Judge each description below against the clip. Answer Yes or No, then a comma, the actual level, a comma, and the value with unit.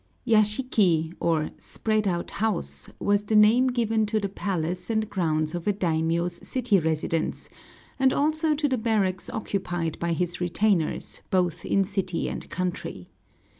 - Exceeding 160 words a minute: No, average, 145 wpm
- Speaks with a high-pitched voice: Yes, high, 195 Hz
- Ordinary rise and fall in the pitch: Yes, average, 4.2 semitones